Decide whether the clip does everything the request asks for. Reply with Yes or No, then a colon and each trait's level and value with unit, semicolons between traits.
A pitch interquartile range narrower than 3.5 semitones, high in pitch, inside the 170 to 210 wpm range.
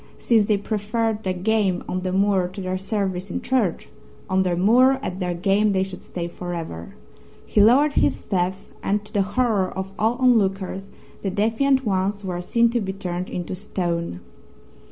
Yes: average, 2.8 semitones; high, 195 Hz; average, 180 wpm